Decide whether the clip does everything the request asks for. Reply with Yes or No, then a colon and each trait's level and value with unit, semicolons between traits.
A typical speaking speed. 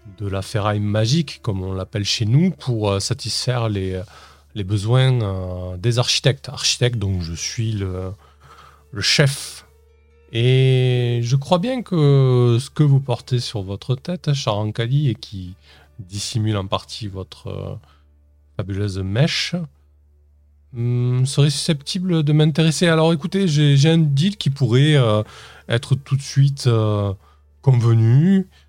No: slow, 130 wpm